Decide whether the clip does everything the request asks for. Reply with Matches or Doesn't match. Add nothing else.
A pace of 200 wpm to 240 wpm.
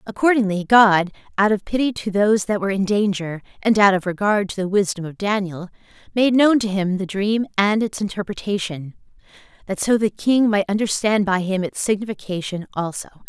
Doesn't match